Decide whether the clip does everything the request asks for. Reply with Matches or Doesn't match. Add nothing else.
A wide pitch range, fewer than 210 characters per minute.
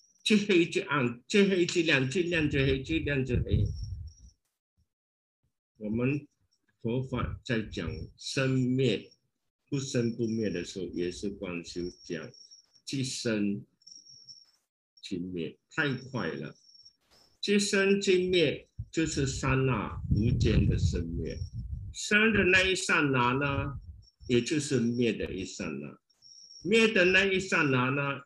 Matches